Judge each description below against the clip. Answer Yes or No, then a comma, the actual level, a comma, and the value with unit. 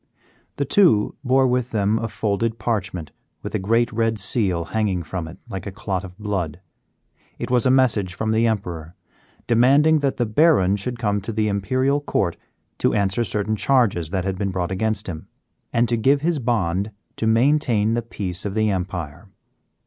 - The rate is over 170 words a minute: Yes, average, 180 wpm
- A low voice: Yes, low, 110 Hz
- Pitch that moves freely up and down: No, average, 3.9 semitones